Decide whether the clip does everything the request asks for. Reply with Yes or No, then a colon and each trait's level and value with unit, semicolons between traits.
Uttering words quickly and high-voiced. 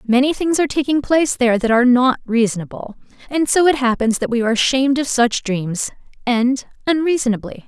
No: average, 180 wpm; very high, 255 Hz